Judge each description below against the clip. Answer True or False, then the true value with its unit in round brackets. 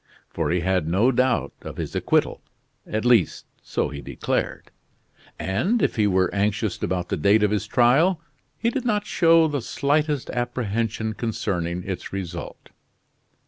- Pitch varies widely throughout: True (6.2 semitones)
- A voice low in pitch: True (110 Hz)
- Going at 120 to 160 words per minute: True (150 wpm)